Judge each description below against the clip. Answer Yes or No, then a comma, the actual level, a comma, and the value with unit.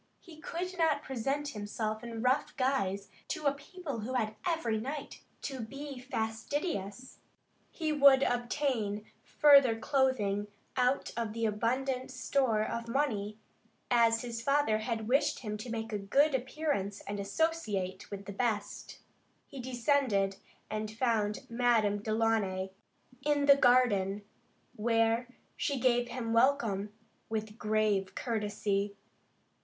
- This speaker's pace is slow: Yes, slow, 130 wpm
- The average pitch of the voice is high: Yes, high, 230 Hz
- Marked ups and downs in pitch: No, average, 4.3 semitones